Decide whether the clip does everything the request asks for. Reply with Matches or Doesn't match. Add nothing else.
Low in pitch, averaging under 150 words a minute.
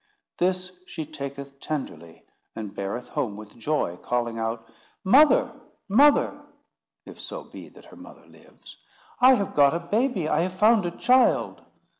Doesn't match